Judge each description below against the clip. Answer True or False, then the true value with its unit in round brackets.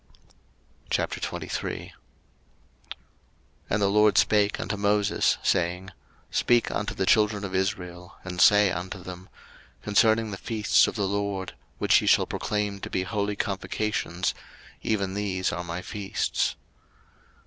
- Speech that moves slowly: True (130 wpm)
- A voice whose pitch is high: False (100 Hz)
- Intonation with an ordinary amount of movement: False (2.0 semitones)